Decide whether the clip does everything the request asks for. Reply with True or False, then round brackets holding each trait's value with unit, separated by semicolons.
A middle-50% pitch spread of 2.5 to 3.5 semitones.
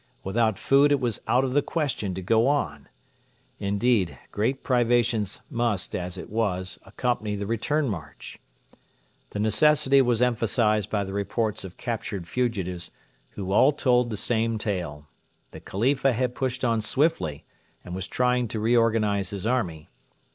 False (3.9 semitones)